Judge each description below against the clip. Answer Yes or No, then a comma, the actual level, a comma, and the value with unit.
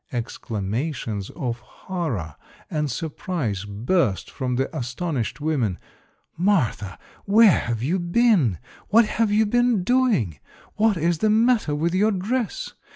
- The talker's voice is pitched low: No, medium, 160 Hz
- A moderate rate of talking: No, slow, 125 wpm